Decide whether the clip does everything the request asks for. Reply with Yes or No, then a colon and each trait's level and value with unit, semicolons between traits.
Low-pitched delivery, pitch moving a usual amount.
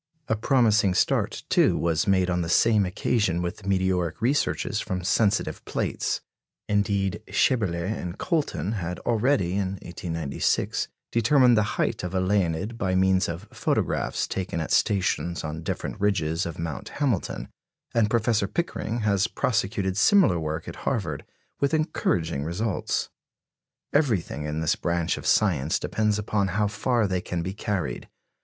Yes: very low, 95 Hz; average, 4.0 semitones